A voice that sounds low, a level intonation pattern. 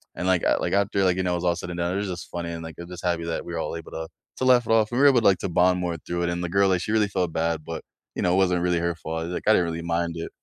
Yes: very low, 90 Hz; narrow, 1.8 semitones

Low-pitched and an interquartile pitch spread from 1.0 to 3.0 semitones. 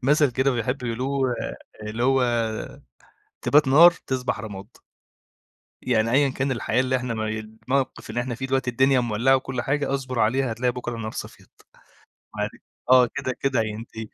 Yes: low, 125 Hz; average, 2.7 semitones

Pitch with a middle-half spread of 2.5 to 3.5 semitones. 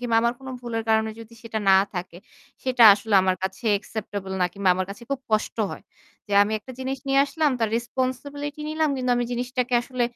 No: average, 3.9 semitones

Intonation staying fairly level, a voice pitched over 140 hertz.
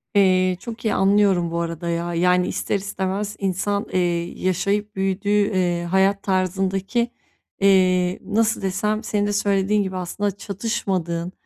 Yes: narrow, 2.1 semitones; high, 190 Hz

